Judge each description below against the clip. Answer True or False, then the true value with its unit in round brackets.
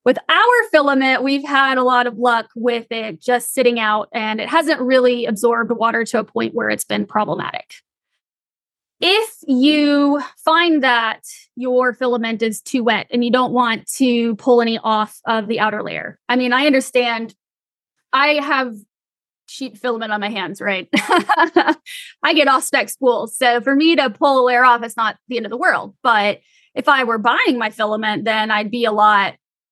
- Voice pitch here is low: False (245 Hz)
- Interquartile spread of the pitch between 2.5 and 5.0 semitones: True (3.4 semitones)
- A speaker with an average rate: True (185 wpm)